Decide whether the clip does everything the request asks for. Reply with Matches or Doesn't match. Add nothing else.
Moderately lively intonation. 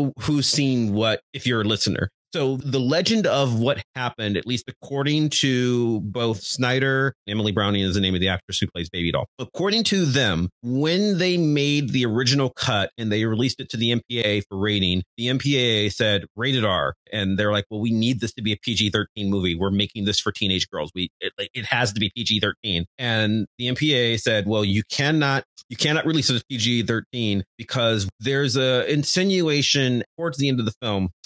Matches